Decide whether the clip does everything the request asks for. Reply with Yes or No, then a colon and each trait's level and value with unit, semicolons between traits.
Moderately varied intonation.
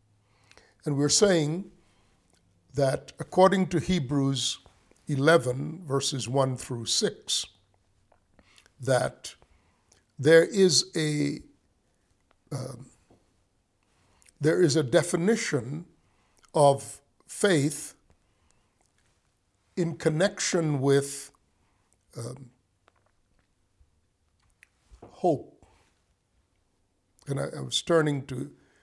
No: wide, 8.0 semitones